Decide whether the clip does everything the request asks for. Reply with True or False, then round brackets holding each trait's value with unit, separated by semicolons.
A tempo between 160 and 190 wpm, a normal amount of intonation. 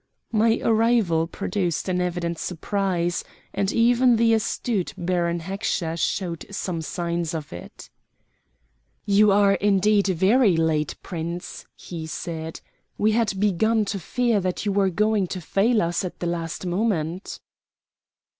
False (135 wpm; 3.8 semitones)